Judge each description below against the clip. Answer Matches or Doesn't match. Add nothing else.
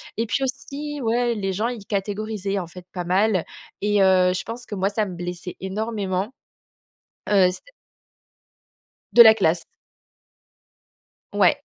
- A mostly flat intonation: Doesn't match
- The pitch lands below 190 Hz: Doesn't match